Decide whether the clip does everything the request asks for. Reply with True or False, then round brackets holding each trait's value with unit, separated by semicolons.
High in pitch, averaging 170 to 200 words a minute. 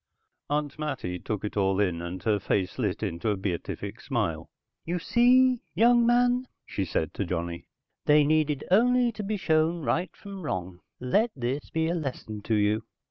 False (145 Hz; 175 wpm)